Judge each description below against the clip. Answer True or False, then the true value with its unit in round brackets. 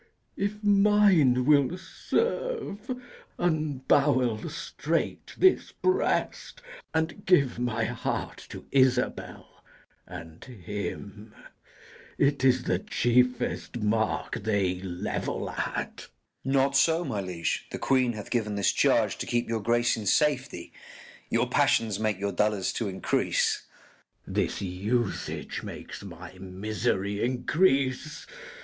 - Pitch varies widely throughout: True (6.0 semitones)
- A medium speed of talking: False (115 wpm)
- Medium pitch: False (120 Hz)